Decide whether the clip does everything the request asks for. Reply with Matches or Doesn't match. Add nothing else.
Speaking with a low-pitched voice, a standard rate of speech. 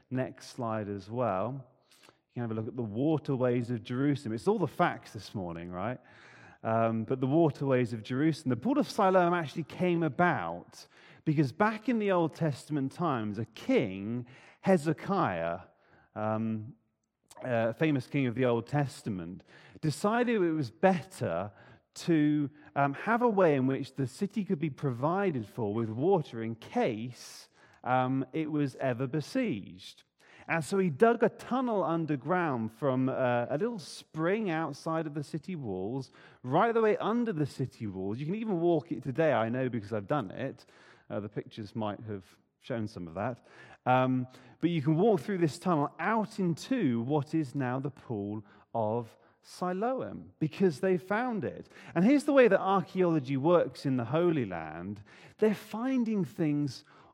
Doesn't match